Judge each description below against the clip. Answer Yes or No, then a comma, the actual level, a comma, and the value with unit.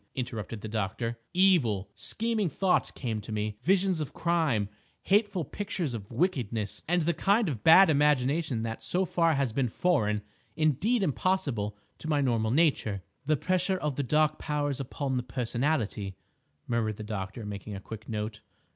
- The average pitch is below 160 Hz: Yes, low, 135 Hz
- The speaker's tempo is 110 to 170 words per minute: Yes, average, 160 wpm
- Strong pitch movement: Yes, wide, 7.4 semitones